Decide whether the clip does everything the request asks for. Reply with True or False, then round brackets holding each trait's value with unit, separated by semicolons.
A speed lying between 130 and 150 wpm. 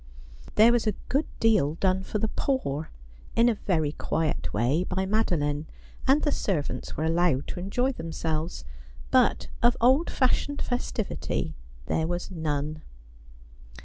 True (140 wpm)